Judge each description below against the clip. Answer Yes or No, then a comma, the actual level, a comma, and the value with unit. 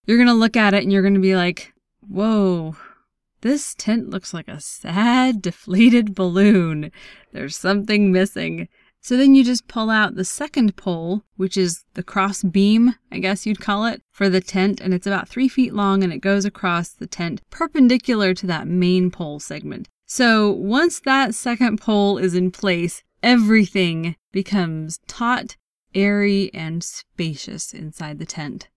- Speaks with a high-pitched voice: Yes, high, 195 Hz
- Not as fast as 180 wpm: Yes, average, 165 wpm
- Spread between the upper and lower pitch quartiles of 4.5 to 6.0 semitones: No, average, 3.6 semitones